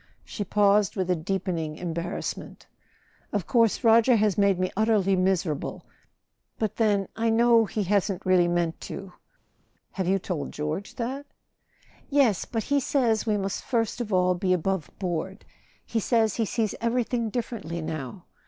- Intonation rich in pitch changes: No, average, 3.8 semitones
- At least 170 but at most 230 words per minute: No, average, 150 wpm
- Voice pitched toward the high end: Yes, high, 200 Hz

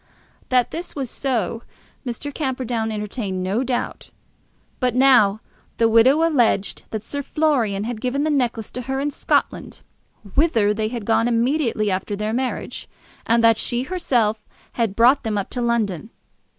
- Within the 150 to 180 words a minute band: Yes, average, 155 wpm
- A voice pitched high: Yes, high, 235 Hz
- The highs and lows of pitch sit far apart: No, average, 3.5 semitones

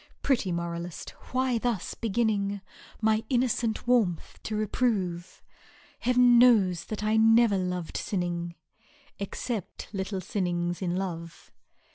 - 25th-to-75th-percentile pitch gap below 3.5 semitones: No, average, 4.7 semitones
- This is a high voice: Yes, high, 200 Hz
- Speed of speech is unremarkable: No, slow, 115 wpm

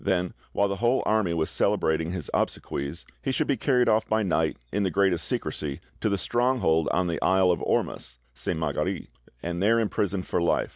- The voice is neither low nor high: No, very low, 95 Hz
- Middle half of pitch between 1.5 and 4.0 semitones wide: No, average, 4.6 semitones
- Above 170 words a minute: Yes, average, 195 wpm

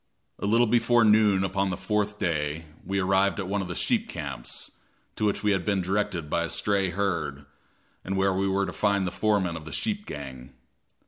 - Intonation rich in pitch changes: No, average, 3.3 semitones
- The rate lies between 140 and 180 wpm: No, fast, 205 wpm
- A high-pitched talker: No, very low, 95 Hz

